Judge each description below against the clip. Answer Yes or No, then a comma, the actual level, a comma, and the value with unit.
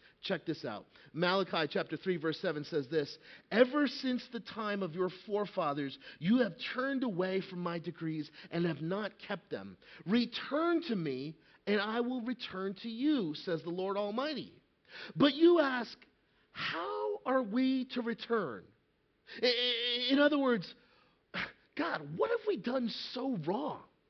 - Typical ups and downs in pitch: No, wide, 6.6 semitones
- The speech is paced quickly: No, average, 150 wpm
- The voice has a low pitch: No, high, 210 Hz